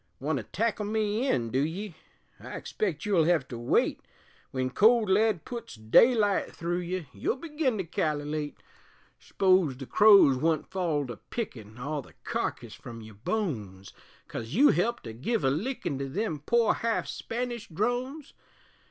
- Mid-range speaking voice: Yes, medium, 175 Hz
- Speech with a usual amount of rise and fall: No, wide, 8.6 semitones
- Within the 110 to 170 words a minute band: Yes, average, 160 wpm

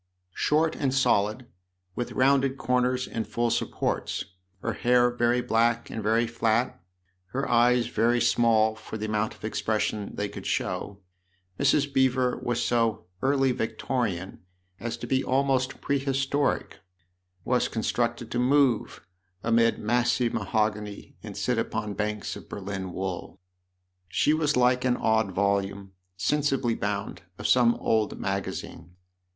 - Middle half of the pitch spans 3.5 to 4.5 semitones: No, average, 3.1 semitones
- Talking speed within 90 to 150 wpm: Yes, average, 140 wpm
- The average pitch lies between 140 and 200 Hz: No, low, 120 Hz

